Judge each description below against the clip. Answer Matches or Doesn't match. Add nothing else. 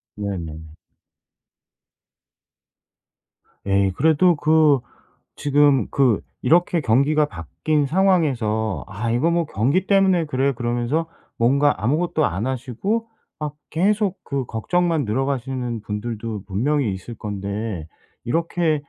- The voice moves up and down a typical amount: Doesn't match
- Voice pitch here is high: Doesn't match